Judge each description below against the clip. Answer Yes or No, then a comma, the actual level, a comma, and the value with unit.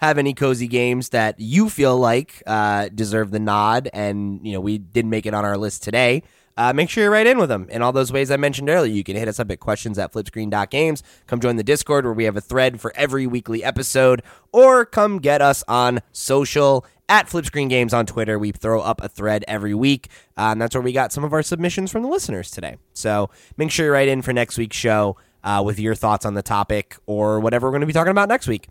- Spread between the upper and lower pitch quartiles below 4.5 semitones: No, average, 4.8 semitones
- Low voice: Yes, low, 120 Hz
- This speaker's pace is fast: Yes, fast, 250 wpm